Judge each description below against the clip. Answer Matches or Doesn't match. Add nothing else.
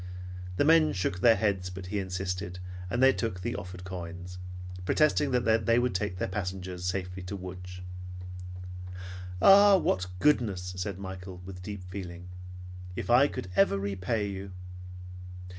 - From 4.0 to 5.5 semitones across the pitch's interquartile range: Doesn't match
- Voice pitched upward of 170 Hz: Doesn't match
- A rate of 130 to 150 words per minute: Matches